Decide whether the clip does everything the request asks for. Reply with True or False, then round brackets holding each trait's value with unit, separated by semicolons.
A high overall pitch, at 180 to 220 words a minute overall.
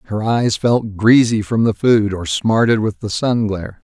False (110 Hz; 200 wpm)